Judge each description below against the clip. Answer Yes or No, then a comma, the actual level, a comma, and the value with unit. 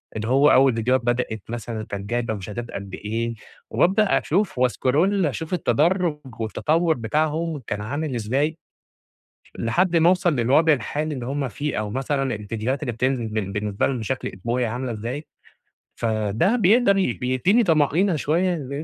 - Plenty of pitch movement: Yes, wide, 5.7 semitones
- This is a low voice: Yes, low, 130 Hz